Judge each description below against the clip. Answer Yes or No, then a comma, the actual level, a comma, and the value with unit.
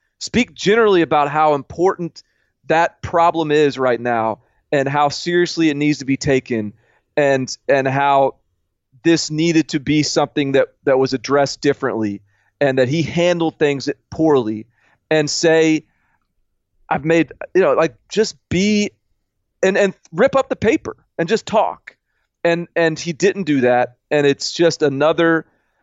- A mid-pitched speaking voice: Yes, medium, 150 Hz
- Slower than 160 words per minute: Yes, average, 150 wpm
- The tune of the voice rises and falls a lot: No, average, 3.9 semitones